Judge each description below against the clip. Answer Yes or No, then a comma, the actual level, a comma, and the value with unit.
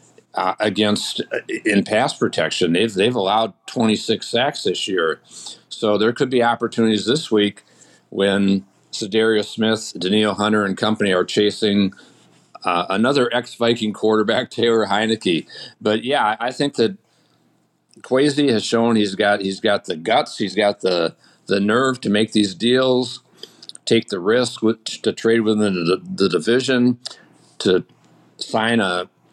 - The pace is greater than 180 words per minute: No, average, 145 wpm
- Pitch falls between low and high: No, low, 110 Hz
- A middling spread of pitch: No, narrow, 2.2 semitones